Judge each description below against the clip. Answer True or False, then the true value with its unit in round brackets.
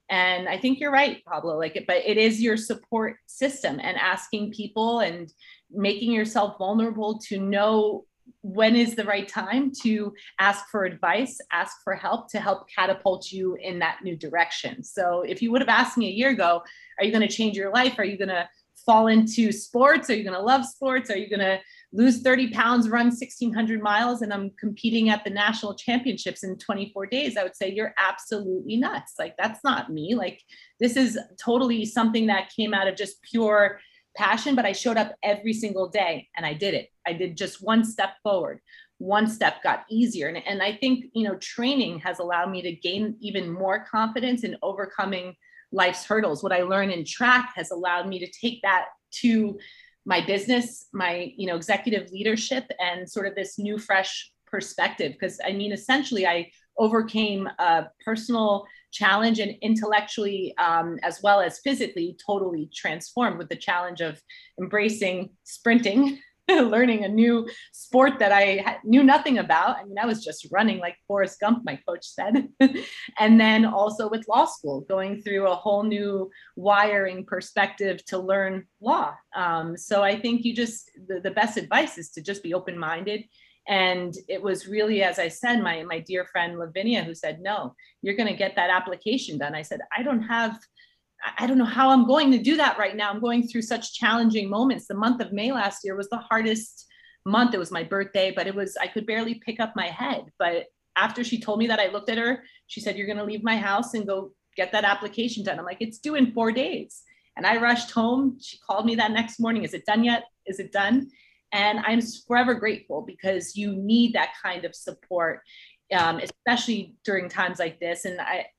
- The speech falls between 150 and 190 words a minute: False (200 wpm)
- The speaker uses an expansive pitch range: False (3.5 semitones)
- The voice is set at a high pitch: True (210 Hz)